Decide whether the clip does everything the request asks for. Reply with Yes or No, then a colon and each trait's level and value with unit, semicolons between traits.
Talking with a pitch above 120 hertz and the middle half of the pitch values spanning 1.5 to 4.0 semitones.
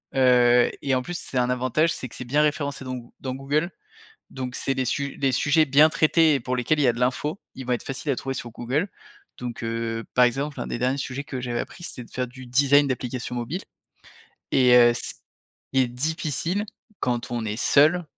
Yes: low, 130 Hz; average, 2.8 semitones